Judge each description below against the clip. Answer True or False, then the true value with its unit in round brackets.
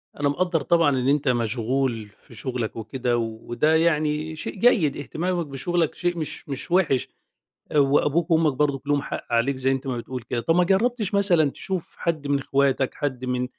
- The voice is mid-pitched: True (145 Hz)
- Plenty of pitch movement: False (4.4 semitones)